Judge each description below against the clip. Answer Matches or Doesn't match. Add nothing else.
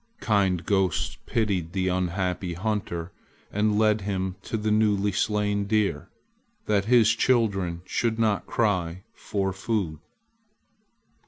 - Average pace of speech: Doesn't match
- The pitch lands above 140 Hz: Doesn't match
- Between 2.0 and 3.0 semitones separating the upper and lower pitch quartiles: Matches